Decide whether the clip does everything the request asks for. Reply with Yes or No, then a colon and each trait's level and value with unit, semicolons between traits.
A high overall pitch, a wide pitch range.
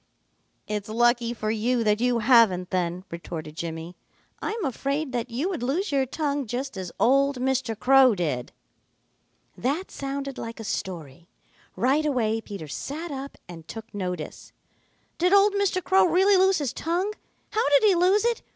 Yes: very high, 250 Hz; wide, 6.6 semitones